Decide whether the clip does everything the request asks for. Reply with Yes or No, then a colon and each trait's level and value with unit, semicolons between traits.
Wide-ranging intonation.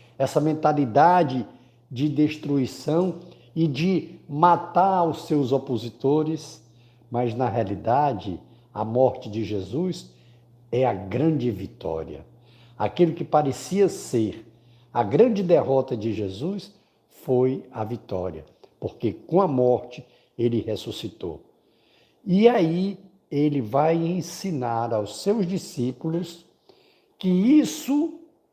Yes: wide, 6.3 semitones